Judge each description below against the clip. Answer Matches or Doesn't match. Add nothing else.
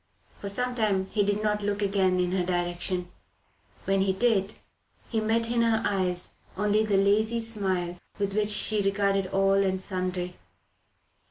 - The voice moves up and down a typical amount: Doesn't match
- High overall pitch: Matches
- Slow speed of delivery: Doesn't match